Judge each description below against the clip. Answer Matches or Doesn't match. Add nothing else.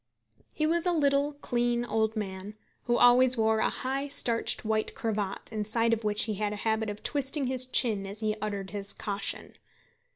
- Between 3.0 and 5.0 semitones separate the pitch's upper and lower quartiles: Matches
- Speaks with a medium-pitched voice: Doesn't match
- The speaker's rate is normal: Matches